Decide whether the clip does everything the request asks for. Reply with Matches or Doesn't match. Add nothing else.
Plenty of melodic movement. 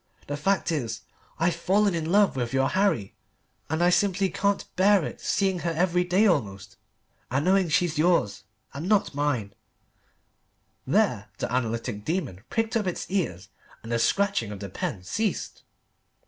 Matches